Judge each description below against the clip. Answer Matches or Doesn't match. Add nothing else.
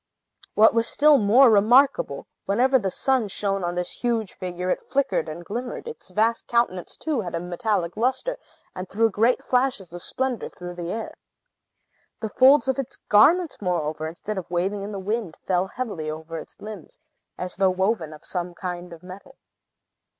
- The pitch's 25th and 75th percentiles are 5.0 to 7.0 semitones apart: Matches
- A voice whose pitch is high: Matches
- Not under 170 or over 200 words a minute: Matches